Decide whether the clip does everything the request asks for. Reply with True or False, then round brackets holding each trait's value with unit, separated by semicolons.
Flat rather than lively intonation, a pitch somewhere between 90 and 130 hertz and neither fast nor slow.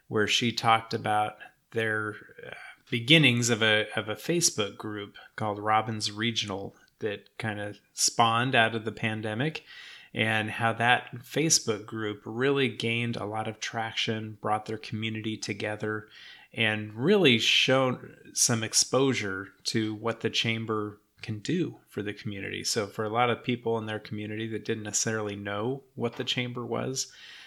True (2.2 semitones; 110 Hz; 150 wpm)